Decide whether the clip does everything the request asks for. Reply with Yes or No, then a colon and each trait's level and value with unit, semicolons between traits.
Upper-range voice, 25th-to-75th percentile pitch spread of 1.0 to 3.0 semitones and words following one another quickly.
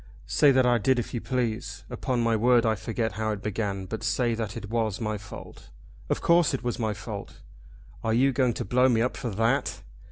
No: low, 115 Hz; narrow, 2.5 semitones; fast, 220 wpm